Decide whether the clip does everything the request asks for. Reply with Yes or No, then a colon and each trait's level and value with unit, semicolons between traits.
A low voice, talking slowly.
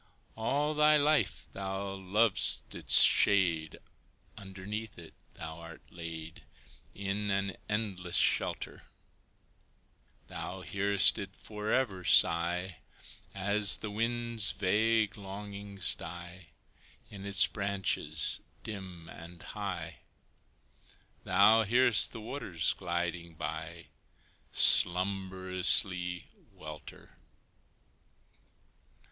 Yes: very low, 95 Hz; slow, 85 wpm